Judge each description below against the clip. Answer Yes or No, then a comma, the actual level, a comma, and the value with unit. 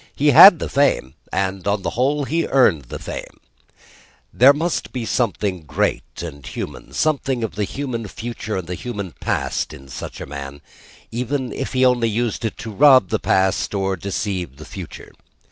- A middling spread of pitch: No, wide, 5.8 semitones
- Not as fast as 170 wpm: No, average, 180 wpm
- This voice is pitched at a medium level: No, low, 110 Hz